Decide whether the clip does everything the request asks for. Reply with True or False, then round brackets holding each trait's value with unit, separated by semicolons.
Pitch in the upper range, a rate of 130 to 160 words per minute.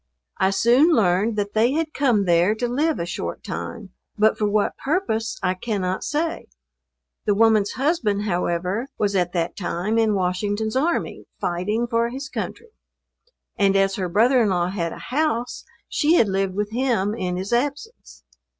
False (215 Hz; 170 wpm)